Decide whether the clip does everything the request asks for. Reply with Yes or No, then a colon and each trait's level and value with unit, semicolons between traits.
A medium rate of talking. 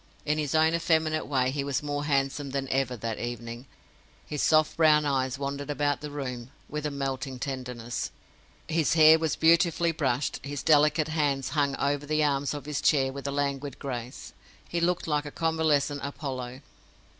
Yes: average, 175 wpm